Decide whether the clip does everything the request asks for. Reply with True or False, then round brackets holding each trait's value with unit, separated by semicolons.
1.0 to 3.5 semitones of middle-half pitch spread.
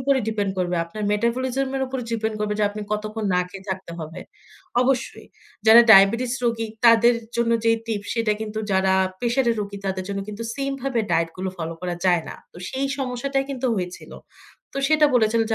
False (4.2 semitones)